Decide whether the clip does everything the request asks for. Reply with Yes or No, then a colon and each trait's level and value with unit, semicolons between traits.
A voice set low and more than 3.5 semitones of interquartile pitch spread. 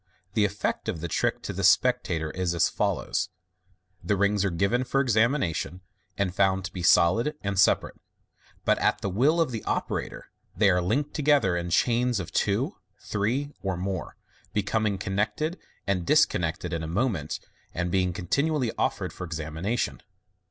Yes: low, 100 Hz; average, 4.9 semitones